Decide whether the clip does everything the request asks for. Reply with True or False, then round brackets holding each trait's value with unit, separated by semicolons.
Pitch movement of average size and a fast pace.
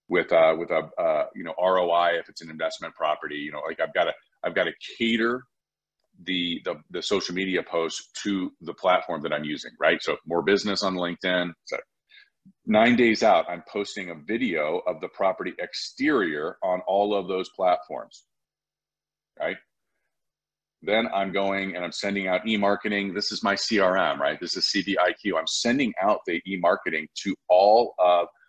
False (3.6 semitones; 175 wpm)